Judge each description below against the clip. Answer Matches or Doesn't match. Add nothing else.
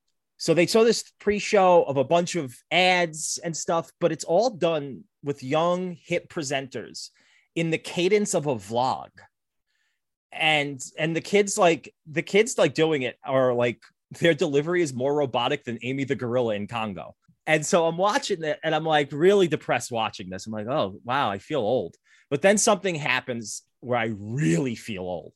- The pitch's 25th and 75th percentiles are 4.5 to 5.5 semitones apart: Matches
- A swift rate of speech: Doesn't match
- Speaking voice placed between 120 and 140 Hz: Doesn't match